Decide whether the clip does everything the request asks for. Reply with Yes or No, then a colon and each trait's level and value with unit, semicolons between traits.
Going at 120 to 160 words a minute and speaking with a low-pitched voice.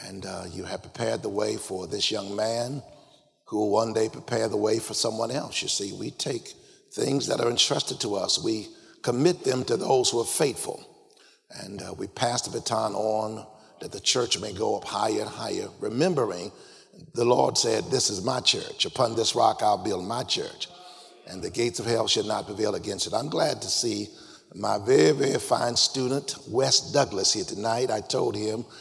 No: average, 200 wpm; low, 120 Hz